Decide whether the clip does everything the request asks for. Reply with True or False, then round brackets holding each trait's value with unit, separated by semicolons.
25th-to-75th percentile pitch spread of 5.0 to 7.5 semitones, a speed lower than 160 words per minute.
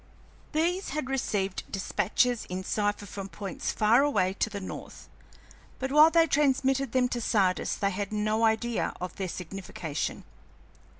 True (5.4 semitones; 145 wpm)